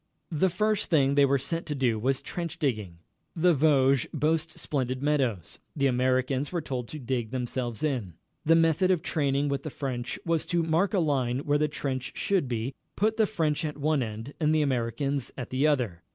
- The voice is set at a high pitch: No, medium, 140 Hz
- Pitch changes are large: No, average, 3.7 semitones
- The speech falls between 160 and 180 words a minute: No, average, 195 wpm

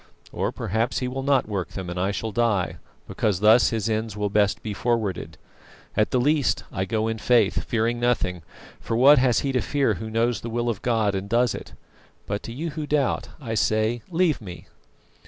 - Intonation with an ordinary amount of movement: Yes, average, 3.1 semitones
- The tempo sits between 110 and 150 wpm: No, fast, 205 wpm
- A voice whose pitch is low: Yes, low, 115 Hz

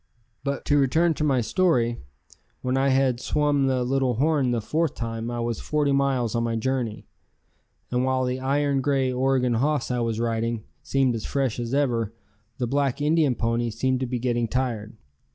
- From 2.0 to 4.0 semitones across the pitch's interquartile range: Yes, average, 2.7 semitones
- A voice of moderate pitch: No, low, 130 Hz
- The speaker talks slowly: No, average, 185 wpm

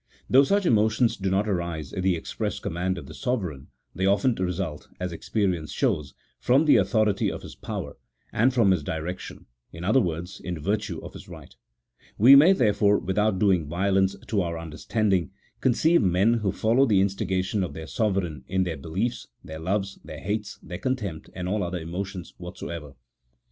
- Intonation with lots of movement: No, average, 3.8 semitones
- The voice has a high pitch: No, very low, 95 Hz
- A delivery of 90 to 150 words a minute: No, average, 185 wpm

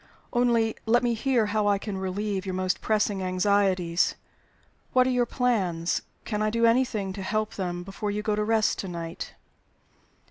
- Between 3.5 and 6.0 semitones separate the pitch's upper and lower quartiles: No, average, 3.1 semitones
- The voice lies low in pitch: No, high, 210 Hz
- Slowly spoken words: No, average, 175 wpm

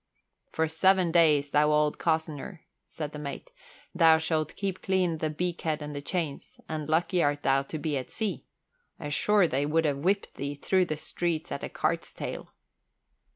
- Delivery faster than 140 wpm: Yes, average, 175 wpm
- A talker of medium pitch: Yes, medium, 160 Hz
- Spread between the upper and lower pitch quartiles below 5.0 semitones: Yes, average, 2.9 semitones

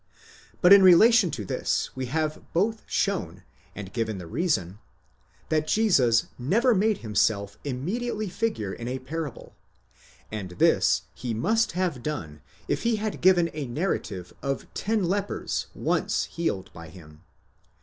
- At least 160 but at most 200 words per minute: No, average, 140 wpm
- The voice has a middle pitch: Yes, medium, 150 Hz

